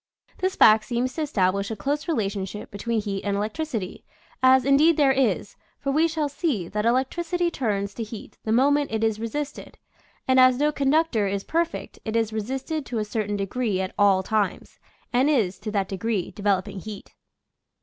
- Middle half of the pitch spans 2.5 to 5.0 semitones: No, wide, 5.4 semitones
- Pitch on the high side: Yes, high, 225 Hz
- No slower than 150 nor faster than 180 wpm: No, average, 190 wpm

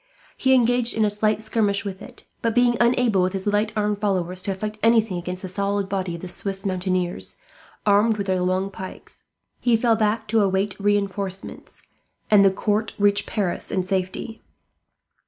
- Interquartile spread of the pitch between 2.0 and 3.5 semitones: Yes, narrow, 2.5 semitones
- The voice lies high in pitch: Yes, high, 200 Hz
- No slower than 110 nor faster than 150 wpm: No, average, 175 wpm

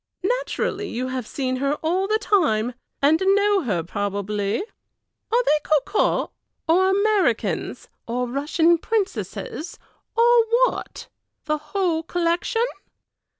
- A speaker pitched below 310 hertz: No, very high, 335 Hz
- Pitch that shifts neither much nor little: No, wide, 8.0 semitones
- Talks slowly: Yes, slow, 110 wpm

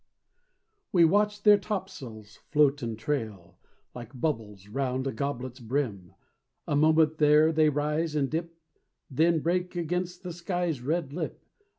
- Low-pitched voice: No, medium, 150 Hz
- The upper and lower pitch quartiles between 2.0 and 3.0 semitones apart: No, average, 5.1 semitones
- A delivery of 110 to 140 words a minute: Yes, slow, 135 wpm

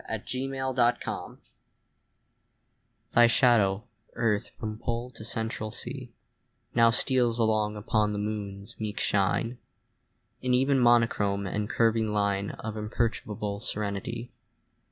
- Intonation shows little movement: Yes, narrow, 2.3 semitones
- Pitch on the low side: Yes, low, 110 Hz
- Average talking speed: No, slow, 115 wpm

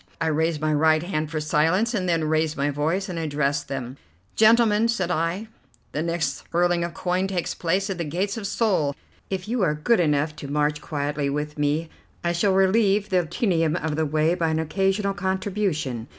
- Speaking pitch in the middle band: Yes, medium, 165 Hz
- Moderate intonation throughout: Yes, average, 4.1 semitones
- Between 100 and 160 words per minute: No, average, 195 wpm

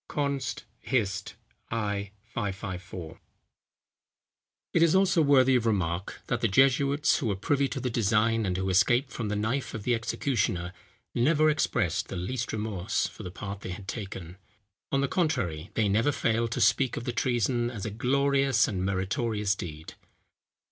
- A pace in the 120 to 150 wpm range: No, average, 160 wpm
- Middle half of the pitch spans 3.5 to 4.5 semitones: No, average, 5.2 semitones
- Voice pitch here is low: Yes, low, 115 Hz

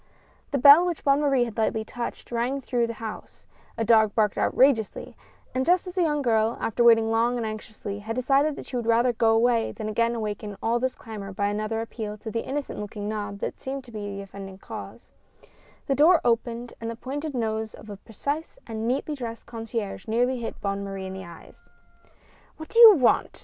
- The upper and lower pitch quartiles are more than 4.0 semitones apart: No, average, 3.2 semitones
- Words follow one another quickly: Yes, fast, 210 wpm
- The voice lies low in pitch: No, high, 230 Hz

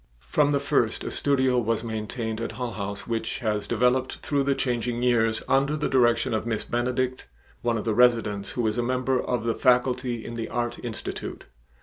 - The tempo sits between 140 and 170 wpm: No, average, 195 wpm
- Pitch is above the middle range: No, low, 120 Hz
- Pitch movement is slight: Yes, narrow, 2.3 semitones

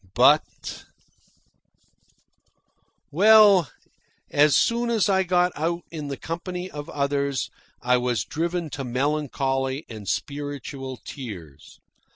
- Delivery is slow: Yes, slow, 105 wpm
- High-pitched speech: No, medium, 145 Hz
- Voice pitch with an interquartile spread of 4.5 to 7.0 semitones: Yes, average, 4.9 semitones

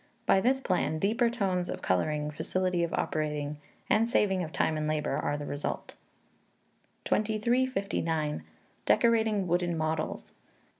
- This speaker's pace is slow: Yes, slow, 130 wpm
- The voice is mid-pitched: Yes, medium, 180 Hz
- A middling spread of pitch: No, wide, 5.7 semitones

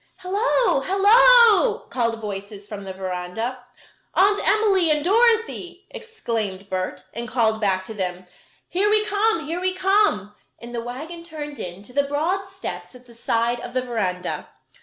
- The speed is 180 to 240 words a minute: No, average, 160 wpm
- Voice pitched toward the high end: Yes, very high, 265 Hz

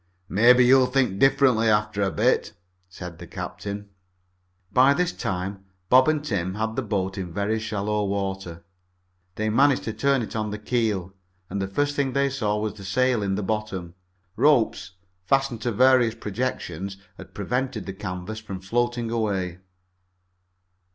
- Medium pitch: No, low, 110 Hz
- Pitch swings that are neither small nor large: Yes, average, 4.5 semitones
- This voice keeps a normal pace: Yes, average, 160 wpm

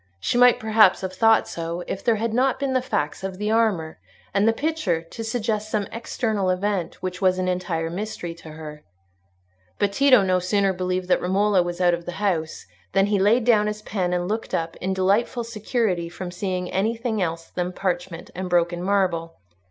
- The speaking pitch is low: No, high, 190 Hz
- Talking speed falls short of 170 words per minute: No, average, 195 wpm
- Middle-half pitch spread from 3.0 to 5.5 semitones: Yes, average, 3.6 semitones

